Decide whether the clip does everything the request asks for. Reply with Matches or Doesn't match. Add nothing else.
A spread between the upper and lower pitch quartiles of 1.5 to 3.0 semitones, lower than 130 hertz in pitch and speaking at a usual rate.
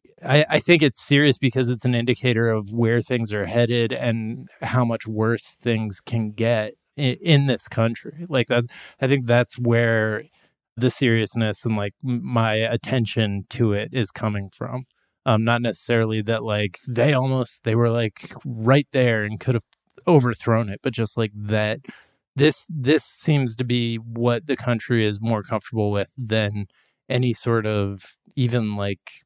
Matches